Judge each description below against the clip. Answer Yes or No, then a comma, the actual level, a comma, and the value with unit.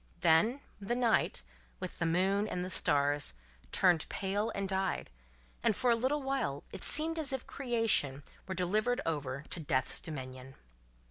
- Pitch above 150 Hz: Yes, high, 190 Hz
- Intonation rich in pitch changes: Yes, wide, 8.4 semitones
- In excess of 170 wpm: No, average, 155 wpm